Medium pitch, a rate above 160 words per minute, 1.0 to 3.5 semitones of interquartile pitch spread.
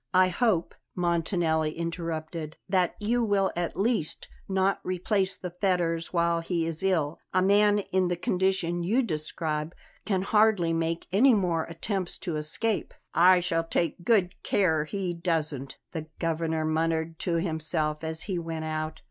No: medium, 170 Hz; average, 150 wpm; average, 2.8 semitones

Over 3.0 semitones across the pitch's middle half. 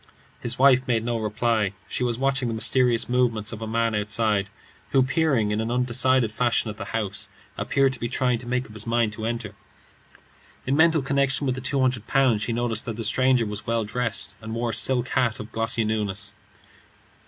No: average, 2.7 semitones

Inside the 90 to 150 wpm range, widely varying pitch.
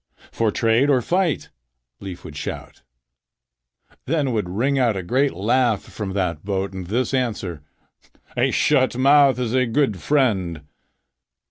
Yes: average, 140 wpm; wide, 5.7 semitones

